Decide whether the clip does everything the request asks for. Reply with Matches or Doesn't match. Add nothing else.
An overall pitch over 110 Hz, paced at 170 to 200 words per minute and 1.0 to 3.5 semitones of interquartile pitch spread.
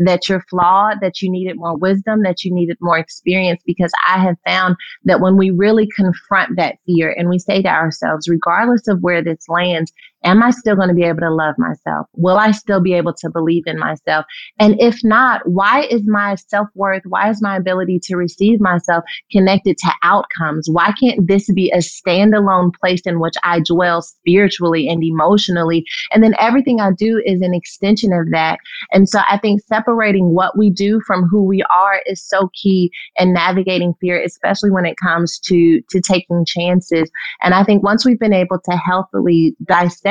Matches